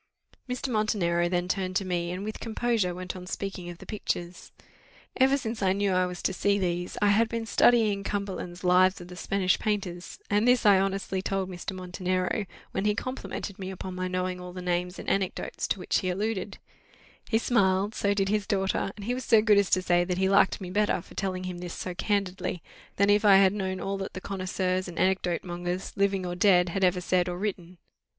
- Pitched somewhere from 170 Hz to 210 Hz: Yes, high, 190 Hz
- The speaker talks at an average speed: No, fast, 215 wpm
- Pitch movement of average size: No, narrow, 2.0 semitones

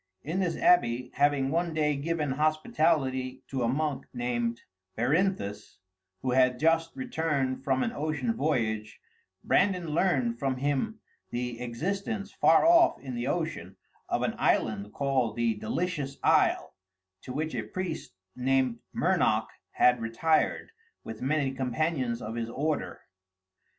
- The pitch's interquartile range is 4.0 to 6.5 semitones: Yes, average, 4.7 semitones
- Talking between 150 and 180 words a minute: No, slow, 135 wpm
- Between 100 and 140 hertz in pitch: Yes, low, 135 Hz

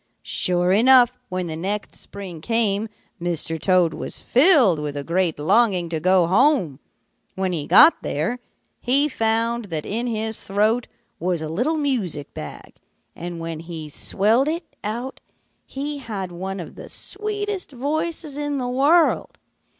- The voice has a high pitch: Yes, high, 205 Hz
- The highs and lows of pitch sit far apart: Yes, wide, 7.2 semitones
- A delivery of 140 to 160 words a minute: Yes, average, 150 wpm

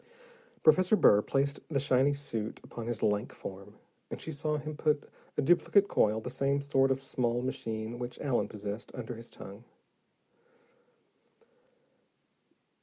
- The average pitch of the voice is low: Yes, low, 130 Hz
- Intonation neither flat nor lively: Yes, average, 4.3 semitones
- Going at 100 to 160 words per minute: Yes, average, 140 wpm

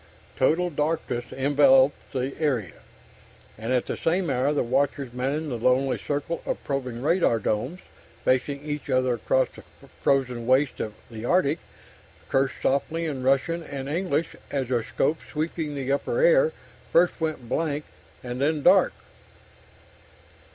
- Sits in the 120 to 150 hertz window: Yes, medium, 140 Hz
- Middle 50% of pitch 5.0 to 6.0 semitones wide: No, average, 3.5 semitones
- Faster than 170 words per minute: No, average, 145 wpm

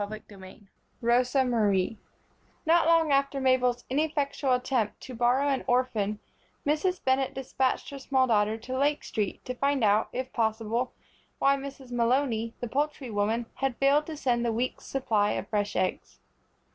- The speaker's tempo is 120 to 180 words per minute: Yes, average, 160 wpm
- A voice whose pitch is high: Yes, very high, 255 Hz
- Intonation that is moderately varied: Yes, average, 3.6 semitones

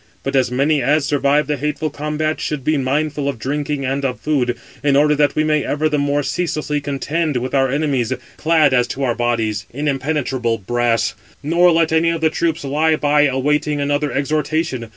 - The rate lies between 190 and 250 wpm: Yes, average, 195 wpm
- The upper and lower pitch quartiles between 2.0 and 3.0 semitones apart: Yes, narrow, 2.4 semitones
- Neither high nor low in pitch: Yes, medium, 145 Hz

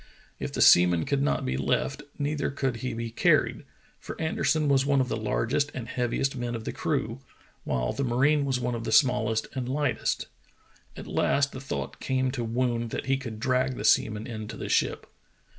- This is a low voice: Yes, low, 125 Hz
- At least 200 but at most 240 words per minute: Yes, fast, 205 wpm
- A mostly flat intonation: No, average, 3.0 semitones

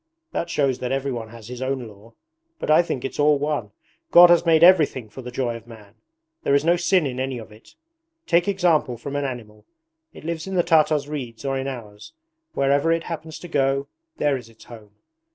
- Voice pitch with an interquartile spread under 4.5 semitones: No, average, 5.0 semitones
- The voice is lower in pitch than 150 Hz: Yes, low, 135 Hz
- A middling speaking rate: No, fast, 210 wpm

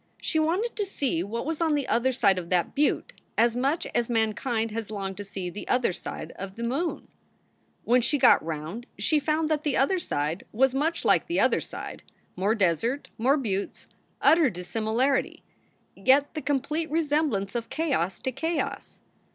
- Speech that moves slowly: No, average, 175 wpm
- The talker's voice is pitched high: Yes, very high, 250 Hz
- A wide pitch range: Yes, wide, 6.7 semitones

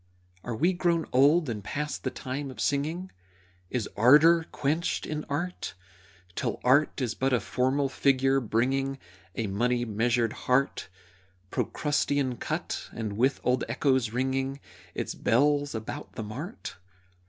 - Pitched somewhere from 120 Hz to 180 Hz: Yes, low, 135 Hz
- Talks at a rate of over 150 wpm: No, slow, 135 wpm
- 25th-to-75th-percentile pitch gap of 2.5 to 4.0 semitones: Yes, average, 3.3 semitones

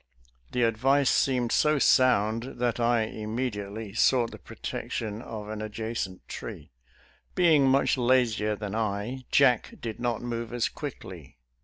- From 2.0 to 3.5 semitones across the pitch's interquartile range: Yes, average, 2.9 semitones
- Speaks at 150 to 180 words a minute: No, average, 140 wpm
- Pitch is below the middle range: Yes, low, 115 Hz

